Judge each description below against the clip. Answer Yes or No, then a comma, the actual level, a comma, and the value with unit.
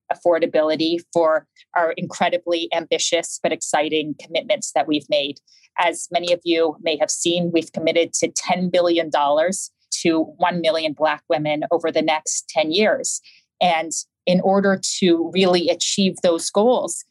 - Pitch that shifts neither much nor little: No, narrow, 2.0 semitones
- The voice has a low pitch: No, medium, 170 Hz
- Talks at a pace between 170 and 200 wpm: No, average, 145 wpm